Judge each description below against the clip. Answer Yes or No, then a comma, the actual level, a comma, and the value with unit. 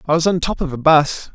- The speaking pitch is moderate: Yes, medium, 155 Hz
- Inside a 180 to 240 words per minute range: No, fast, 310 wpm